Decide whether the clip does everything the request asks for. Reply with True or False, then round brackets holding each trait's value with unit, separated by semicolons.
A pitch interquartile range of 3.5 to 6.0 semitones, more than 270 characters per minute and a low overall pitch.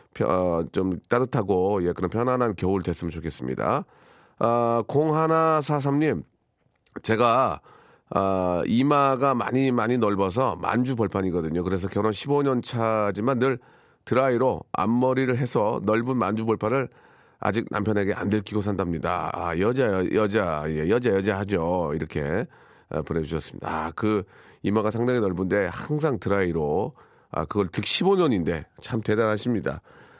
True (5.4 semitones; 295 characters per minute; 105 Hz)